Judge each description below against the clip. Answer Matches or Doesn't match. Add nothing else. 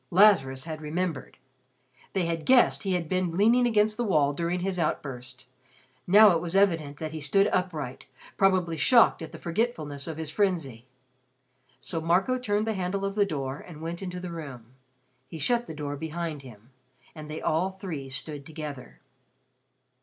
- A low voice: Doesn't match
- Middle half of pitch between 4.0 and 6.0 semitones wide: Matches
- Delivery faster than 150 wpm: Matches